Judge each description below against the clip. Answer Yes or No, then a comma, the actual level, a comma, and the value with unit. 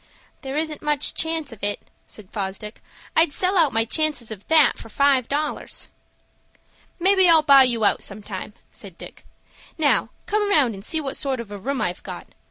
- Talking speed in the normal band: Yes, average, 180 wpm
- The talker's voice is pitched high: Yes, very high, 275 Hz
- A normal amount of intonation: No, wide, 6.3 semitones